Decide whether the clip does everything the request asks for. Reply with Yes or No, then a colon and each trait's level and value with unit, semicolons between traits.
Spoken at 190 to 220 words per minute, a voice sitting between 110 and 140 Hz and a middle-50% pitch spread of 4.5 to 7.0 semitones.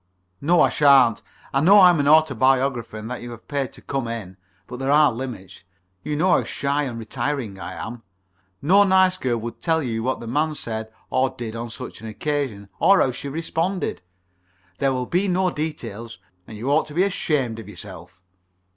Yes: average, 195 wpm; low, 135 Hz; average, 5.0 semitones